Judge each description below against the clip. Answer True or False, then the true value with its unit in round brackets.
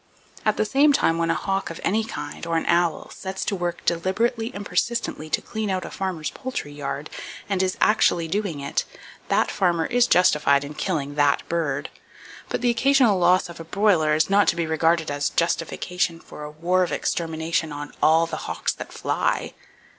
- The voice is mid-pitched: True (170 Hz)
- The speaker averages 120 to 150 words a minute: False (190 wpm)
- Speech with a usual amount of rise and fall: True (3.9 semitones)